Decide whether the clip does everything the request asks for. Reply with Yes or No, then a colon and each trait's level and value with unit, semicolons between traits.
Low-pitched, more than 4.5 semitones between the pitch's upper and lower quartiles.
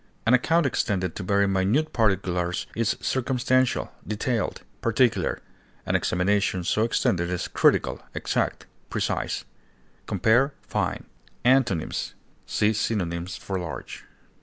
Yes: low, 105 Hz; average, 5.0 semitones